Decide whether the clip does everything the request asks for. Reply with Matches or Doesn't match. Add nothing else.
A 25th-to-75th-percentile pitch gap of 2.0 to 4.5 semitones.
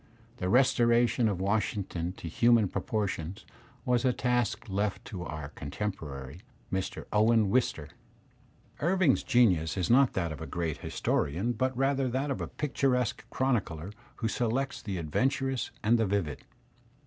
Doesn't match